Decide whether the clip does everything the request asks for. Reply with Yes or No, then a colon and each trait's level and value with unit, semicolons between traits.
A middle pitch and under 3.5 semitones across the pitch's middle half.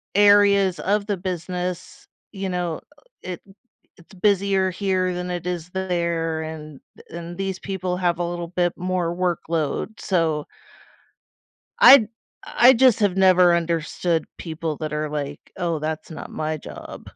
Yes: medium, 180 Hz; narrow, 2.4 semitones